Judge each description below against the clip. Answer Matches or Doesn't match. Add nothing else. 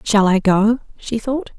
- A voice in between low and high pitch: Doesn't match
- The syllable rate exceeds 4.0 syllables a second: Doesn't match